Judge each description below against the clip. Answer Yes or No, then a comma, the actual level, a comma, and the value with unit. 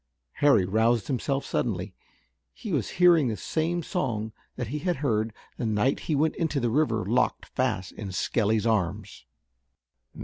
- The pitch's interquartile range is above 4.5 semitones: Yes, wide, 5.5 semitones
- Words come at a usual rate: Yes, average, 150 wpm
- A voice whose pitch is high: No, low, 115 Hz